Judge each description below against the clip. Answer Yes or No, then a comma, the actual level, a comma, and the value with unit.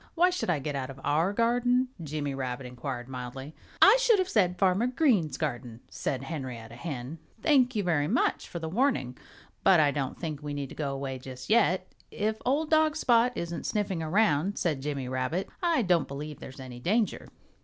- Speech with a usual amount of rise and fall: No, wide, 8.3 semitones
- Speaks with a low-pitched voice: No, medium, 160 Hz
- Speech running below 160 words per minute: No, average, 185 wpm